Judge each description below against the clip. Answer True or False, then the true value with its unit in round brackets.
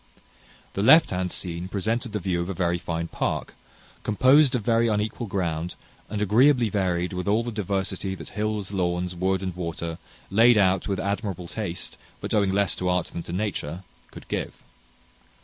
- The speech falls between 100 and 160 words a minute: False (175 wpm)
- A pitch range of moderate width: True (3.2 semitones)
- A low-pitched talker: True (95 Hz)